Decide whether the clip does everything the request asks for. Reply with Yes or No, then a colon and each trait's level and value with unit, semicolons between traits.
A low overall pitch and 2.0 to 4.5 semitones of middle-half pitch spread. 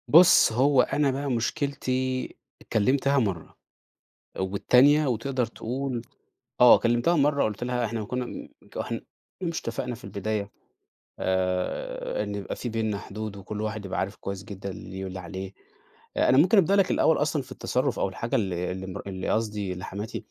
No: low, 115 Hz; average, 5.0 semitones